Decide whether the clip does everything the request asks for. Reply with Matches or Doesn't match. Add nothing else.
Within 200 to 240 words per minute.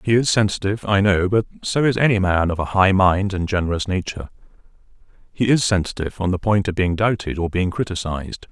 Matches